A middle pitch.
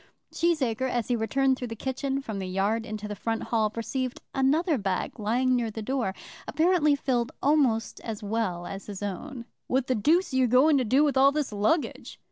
No: high, 245 Hz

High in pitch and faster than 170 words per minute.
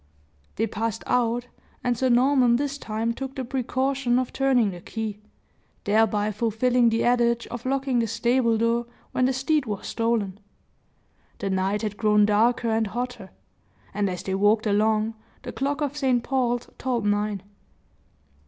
No: high, 235 Hz; average, 155 wpm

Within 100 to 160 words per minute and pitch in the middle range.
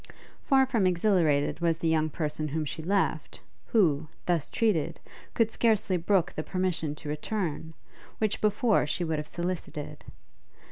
Yes: average, 145 wpm; medium, 170 Hz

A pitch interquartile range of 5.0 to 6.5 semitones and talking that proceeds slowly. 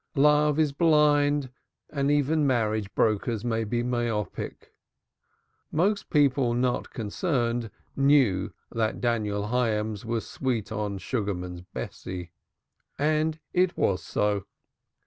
Yes: wide, 5.4 semitones; slow, 110 wpm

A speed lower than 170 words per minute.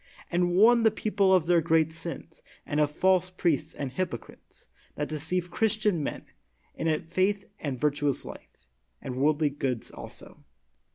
Yes: average, 150 wpm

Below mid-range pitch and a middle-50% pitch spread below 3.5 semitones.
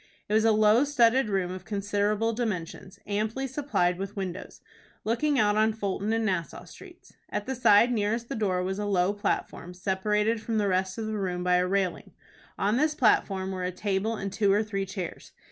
No: high, 205 Hz; average, 2.9 semitones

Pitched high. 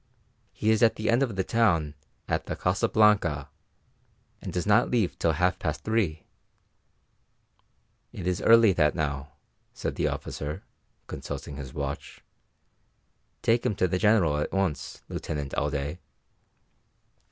No: very low, 90 Hz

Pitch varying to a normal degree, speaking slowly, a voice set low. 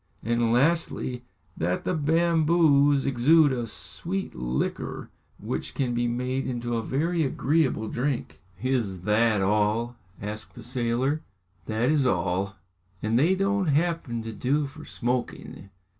Yes: average, 5.0 semitones; slow, 130 wpm; low, 125 Hz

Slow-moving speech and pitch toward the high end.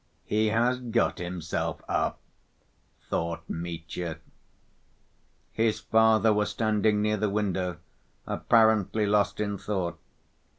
No: slow, 100 wpm; low, 105 Hz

